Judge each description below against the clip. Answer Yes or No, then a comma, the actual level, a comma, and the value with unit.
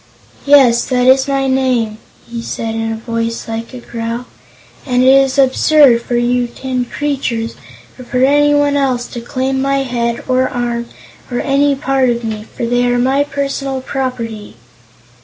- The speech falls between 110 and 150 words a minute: No, average, 165 wpm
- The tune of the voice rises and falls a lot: No, narrow, 2.4 semitones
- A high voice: Yes, very high, 250 Hz